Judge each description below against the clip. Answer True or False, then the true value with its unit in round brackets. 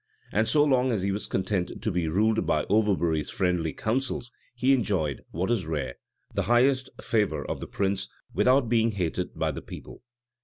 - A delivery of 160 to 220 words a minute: True (180 wpm)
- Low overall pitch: True (105 Hz)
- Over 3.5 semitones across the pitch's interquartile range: True (5.1 semitones)